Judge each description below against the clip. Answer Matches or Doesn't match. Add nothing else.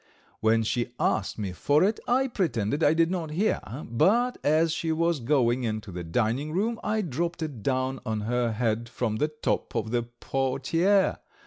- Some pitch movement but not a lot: Doesn't match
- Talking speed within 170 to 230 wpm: Matches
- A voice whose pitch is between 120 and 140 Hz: Matches